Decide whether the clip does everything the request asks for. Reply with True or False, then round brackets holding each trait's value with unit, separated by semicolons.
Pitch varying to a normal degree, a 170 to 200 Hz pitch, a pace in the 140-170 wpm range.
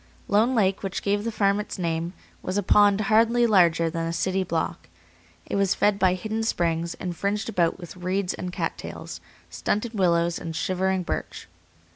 False (3.1 semitones; 190 Hz; 180 wpm)